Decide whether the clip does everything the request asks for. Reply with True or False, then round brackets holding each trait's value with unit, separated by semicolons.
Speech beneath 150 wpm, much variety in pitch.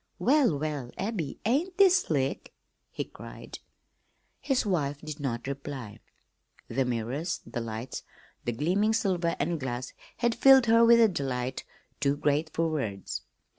True (140 wpm; 8.8 semitones)